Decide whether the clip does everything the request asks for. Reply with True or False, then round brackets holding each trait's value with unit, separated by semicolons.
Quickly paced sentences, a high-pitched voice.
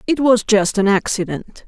False (180 wpm; 210 Hz)